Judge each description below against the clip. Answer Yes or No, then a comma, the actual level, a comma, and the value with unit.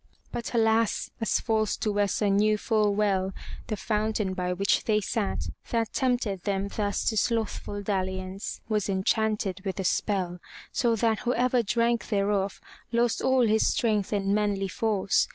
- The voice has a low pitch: No, high, 210 Hz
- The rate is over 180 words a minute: No, average, 155 wpm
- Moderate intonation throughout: No, narrow, 2.3 semitones